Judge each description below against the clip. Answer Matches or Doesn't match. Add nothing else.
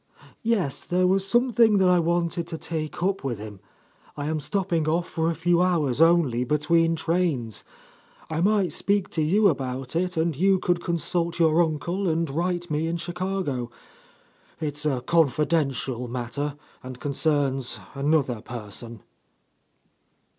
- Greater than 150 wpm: Doesn't match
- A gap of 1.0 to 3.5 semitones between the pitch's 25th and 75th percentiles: Doesn't match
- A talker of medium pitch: Matches